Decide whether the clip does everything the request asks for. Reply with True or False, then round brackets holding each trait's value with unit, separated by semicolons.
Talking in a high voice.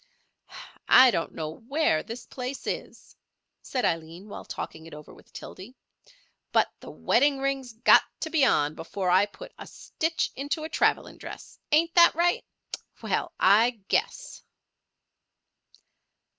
True (245 Hz)